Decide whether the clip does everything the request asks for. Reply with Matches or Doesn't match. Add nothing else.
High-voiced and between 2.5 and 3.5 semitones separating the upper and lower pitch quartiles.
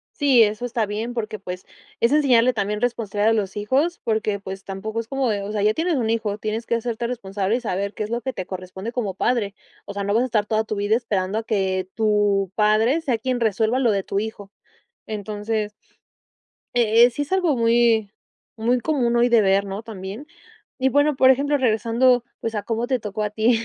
Matches